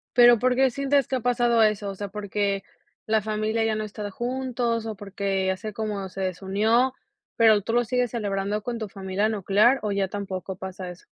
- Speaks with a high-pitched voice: Yes, high, 215 Hz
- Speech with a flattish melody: No, average, 3.2 semitones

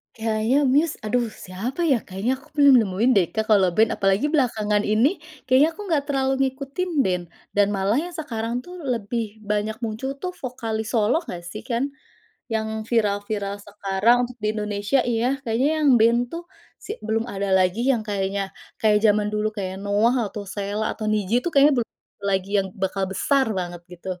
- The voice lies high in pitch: Yes, high, 220 Hz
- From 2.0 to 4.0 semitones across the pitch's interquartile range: No, average, 4.4 semitones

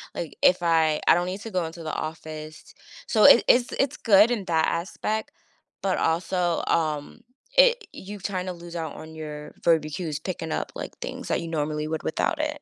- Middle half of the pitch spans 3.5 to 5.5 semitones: Yes, average, 3.8 semitones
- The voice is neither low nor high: Yes, medium, 170 Hz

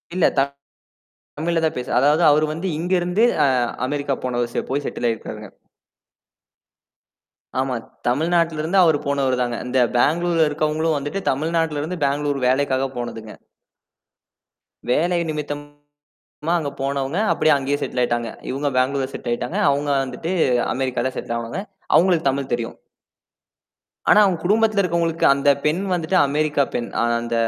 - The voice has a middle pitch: Yes, medium, 145 Hz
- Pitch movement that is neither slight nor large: Yes, average, 3.9 semitones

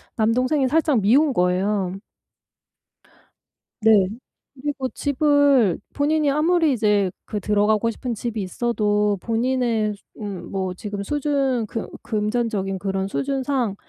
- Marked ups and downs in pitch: No, average, 4.9 semitones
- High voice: Yes, high, 225 Hz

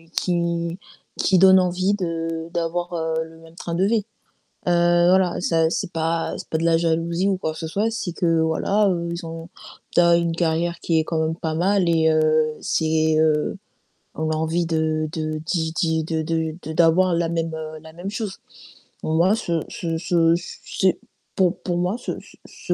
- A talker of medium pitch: Yes, medium, 165 Hz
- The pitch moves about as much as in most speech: No, narrow, 1.6 semitones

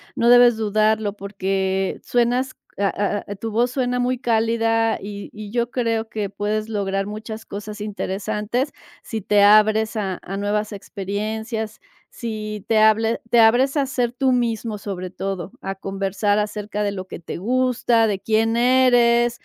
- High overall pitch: Yes, high, 215 Hz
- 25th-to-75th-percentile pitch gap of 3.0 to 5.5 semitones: No, narrow, 2.6 semitones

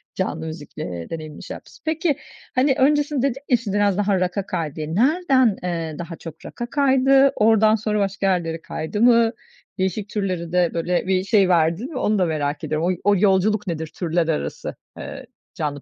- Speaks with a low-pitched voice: No, high, 190 Hz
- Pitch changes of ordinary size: No, wide, 5.7 semitones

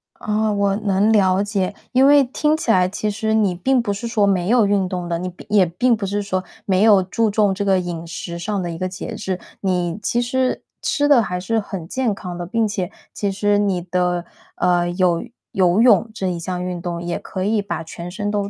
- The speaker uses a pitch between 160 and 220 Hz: Yes, high, 195 Hz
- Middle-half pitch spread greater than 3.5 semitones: No, average, 3.1 semitones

